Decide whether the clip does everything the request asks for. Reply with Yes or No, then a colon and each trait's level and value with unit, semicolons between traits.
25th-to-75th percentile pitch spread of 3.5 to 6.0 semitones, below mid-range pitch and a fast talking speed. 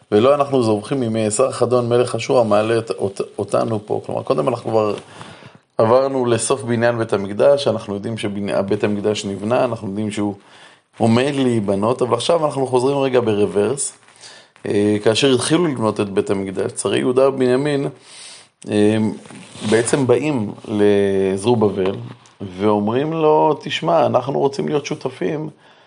No: average, 3.9 semitones; low, 115 Hz; average, 135 wpm